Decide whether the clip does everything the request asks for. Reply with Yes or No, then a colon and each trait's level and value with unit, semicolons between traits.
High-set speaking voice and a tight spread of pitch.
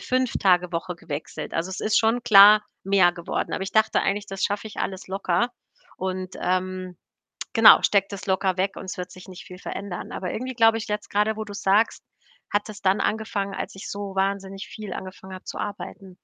Yes: high, 195 Hz; narrow, 2.1 semitones